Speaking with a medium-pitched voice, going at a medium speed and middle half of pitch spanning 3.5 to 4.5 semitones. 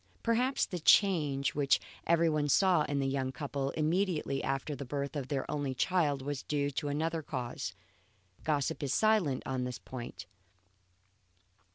No: medium, 145 Hz; average, 150 wpm; average, 3.1 semitones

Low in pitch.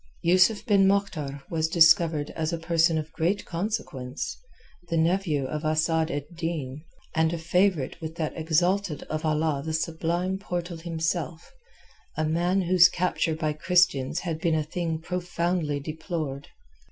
No: medium, 165 Hz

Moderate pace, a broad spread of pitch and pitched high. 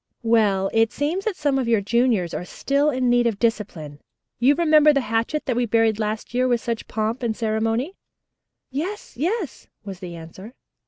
No: average, 180 wpm; average, 4.4 semitones; high, 235 Hz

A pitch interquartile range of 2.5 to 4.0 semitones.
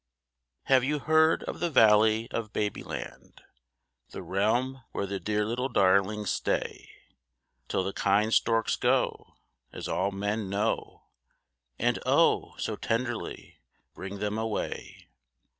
Yes: average, 2.8 semitones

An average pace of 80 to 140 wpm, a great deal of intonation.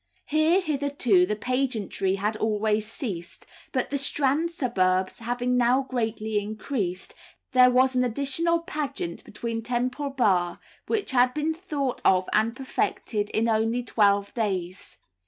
No: slow, 135 wpm; average, 4.5 semitones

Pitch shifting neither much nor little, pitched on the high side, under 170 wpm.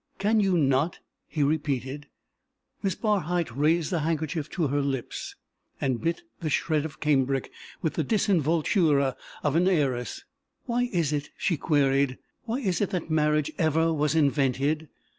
No: average, 3.5 semitones; medium, 155 Hz; average, 150 wpm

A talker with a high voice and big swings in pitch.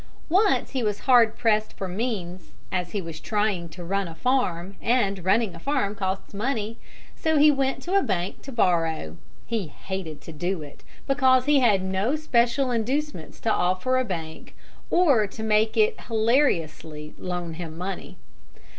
Yes: high, 210 Hz; wide, 6.3 semitones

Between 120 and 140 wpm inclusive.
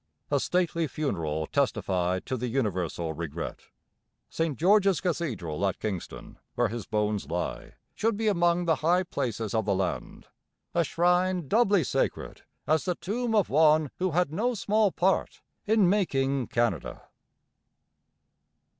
Yes: slow, 135 wpm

